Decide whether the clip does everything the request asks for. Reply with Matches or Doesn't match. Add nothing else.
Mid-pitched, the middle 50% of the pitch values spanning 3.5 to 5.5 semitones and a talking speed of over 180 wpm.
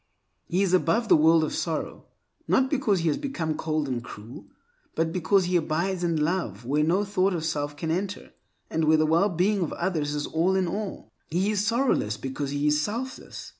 Matches